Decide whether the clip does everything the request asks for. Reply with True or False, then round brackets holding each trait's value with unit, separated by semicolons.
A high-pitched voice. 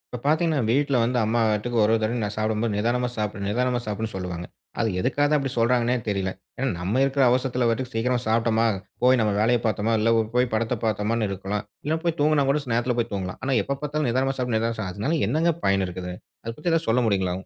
False (115 Hz)